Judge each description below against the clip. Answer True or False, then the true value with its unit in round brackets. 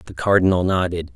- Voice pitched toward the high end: False (90 Hz)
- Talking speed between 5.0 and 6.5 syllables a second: True (6.1 syllables/s)